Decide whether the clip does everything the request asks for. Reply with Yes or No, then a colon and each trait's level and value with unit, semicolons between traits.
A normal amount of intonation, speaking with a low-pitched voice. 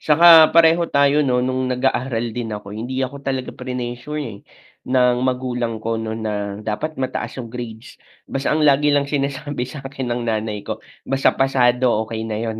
Yes: average, 3.0 semitones; low, 125 Hz